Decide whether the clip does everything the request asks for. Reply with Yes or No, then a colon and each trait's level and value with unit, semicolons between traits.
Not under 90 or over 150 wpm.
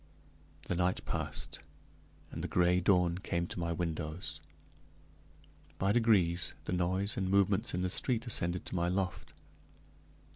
Yes: average, 140 wpm